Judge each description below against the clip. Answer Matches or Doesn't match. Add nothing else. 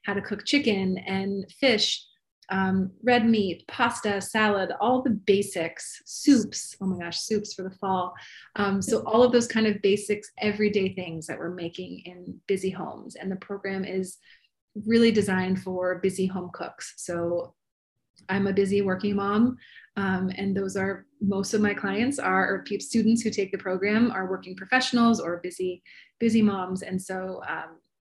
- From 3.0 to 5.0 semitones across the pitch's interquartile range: Doesn't match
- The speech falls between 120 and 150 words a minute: Doesn't match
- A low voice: Doesn't match